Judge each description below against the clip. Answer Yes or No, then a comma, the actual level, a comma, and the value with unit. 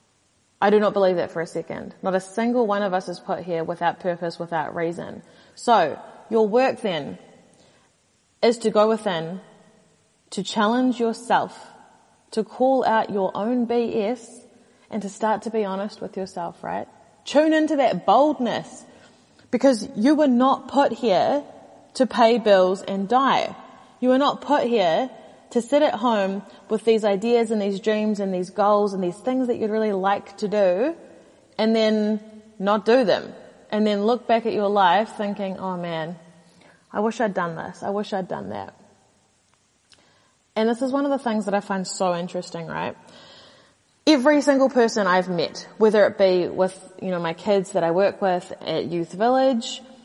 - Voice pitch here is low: No, high, 210 Hz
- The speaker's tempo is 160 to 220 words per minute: Yes, average, 175 wpm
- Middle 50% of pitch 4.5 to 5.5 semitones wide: No, average, 4.0 semitones